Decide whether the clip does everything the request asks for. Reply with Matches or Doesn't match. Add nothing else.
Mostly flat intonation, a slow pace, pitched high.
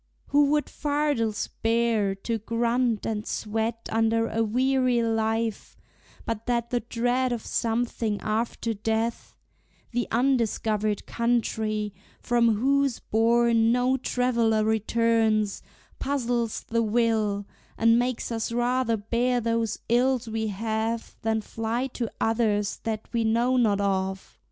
Matches